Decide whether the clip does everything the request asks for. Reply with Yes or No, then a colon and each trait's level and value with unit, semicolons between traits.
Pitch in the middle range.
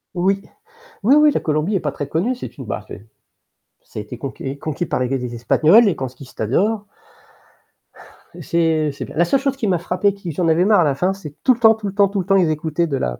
Yes: medium, 170 Hz